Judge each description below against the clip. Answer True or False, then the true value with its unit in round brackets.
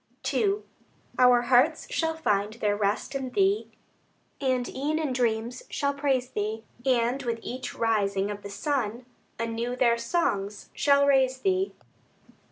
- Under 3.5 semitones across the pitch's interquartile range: False (4.2 semitones)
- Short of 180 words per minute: True (140 wpm)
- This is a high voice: True (250 Hz)